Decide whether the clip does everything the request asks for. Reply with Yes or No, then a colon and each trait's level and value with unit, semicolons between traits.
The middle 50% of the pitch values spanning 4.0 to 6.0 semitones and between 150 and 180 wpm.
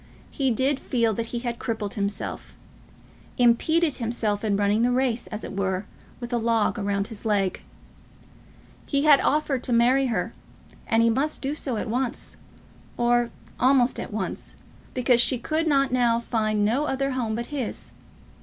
No: average, 3.2 semitones; average, 165 wpm